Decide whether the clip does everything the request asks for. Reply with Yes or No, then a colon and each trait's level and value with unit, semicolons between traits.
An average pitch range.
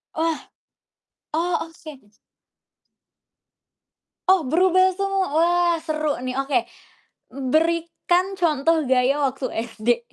Yes: average, 4.4 semitones